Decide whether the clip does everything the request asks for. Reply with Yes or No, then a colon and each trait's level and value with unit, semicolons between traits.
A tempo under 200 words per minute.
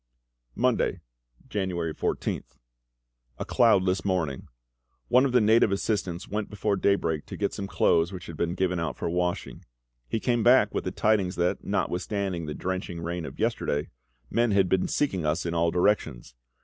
Yes: average, 165 wpm